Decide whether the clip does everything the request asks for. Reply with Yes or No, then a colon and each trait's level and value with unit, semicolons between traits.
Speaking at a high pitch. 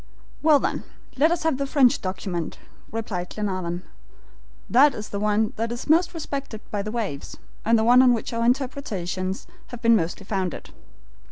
Yes: high, 225 Hz